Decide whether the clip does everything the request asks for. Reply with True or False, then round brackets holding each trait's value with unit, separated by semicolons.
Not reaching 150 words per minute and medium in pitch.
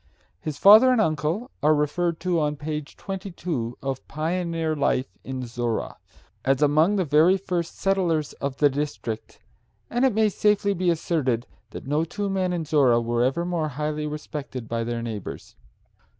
False (165 wpm; 155 Hz)